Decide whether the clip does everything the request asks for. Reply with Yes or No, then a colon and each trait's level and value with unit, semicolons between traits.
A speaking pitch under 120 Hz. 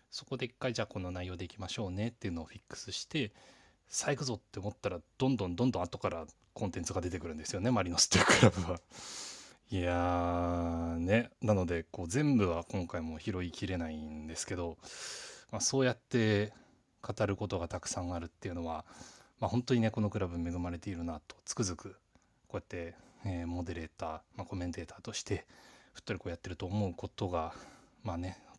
Yes: very low, 95 Hz